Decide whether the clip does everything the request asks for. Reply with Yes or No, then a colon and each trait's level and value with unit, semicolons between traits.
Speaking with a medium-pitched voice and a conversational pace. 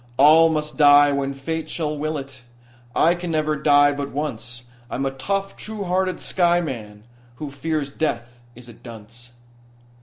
Yes: medium, 145 Hz; average, 160 wpm